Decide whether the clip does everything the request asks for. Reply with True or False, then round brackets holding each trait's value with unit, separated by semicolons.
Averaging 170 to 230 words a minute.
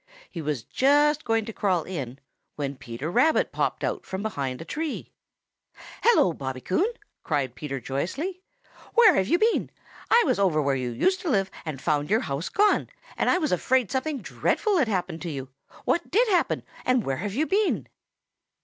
True (185 wpm)